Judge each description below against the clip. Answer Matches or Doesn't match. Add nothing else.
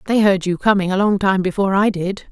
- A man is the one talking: Doesn't match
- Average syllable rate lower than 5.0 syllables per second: Doesn't match